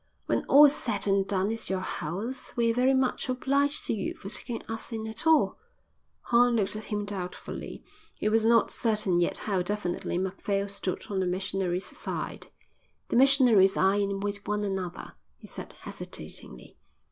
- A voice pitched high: Yes, high, 205 Hz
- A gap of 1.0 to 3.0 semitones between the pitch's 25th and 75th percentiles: No, average, 3.5 semitones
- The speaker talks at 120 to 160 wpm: No, average, 170 wpm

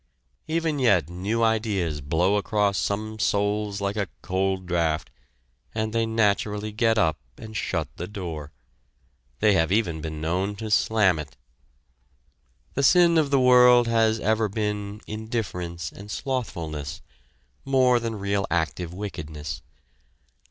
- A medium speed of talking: No, slow, 130 wpm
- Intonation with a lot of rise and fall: No, average, 4.1 semitones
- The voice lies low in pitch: Yes, low, 105 Hz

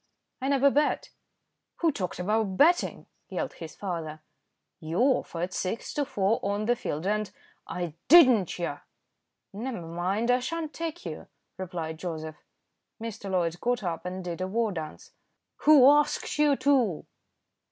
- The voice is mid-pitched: No, high, 200 Hz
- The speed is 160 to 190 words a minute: No, average, 150 wpm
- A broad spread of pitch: Yes, wide, 6.8 semitones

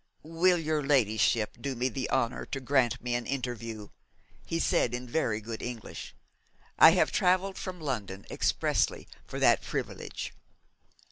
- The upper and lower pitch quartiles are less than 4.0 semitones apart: No, average, 5.0 semitones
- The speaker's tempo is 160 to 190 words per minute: No, average, 145 wpm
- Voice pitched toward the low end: Yes, low, 125 Hz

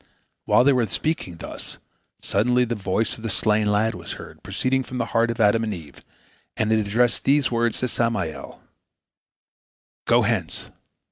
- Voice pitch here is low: Yes, low, 115 Hz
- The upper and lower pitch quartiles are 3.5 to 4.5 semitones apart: No, average, 2.8 semitones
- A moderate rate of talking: Yes, average, 165 wpm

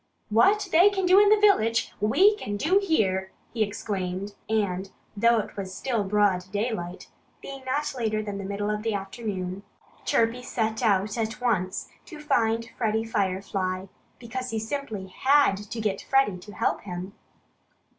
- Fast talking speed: No, average, 160 wpm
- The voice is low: No, high, 220 Hz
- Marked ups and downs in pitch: No, average, 4.3 semitones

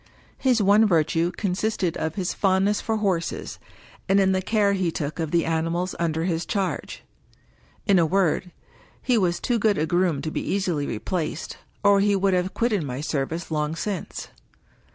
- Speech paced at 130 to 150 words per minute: No, average, 175 wpm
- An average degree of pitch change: Yes, average, 3.5 semitones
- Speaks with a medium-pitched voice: Yes, medium, 180 Hz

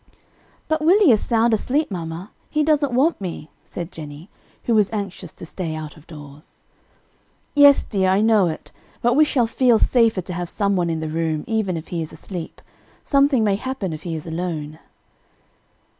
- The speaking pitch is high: Yes, high, 195 Hz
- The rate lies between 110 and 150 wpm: No, average, 185 wpm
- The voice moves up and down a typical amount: No, wide, 6.7 semitones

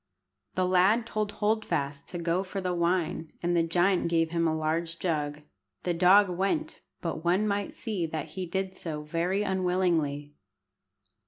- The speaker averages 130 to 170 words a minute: Yes, average, 165 wpm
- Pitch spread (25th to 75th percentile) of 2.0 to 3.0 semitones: Yes, average, 2.7 semitones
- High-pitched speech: No, medium, 175 Hz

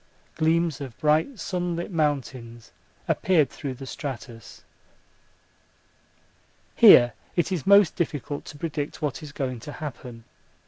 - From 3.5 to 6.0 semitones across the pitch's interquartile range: Yes, average, 4.5 semitones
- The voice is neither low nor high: Yes, medium, 145 Hz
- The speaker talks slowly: Yes, slow, 120 wpm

